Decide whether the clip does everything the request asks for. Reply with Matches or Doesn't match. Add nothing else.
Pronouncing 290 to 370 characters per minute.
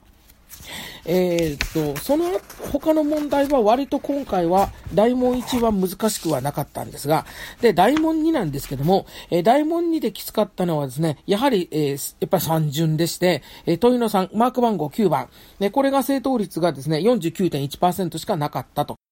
Matches